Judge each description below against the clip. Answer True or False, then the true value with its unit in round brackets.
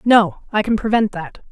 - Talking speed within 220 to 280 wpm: False (200 wpm)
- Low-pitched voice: False (210 Hz)